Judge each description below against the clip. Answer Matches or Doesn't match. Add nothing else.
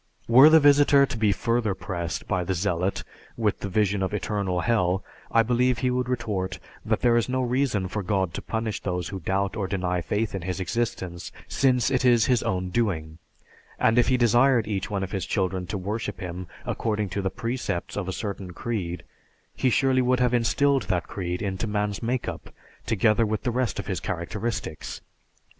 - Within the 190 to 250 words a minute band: Matches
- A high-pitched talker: Doesn't match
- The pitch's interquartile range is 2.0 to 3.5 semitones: Doesn't match